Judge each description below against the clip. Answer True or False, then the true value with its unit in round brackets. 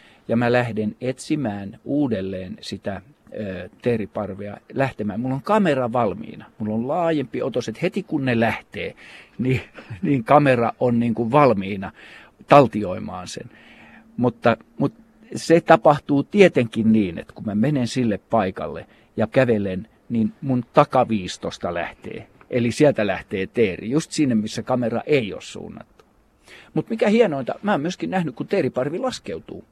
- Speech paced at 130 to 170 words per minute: True (140 wpm)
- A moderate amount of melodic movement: True (5.0 semitones)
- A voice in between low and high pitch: False (125 Hz)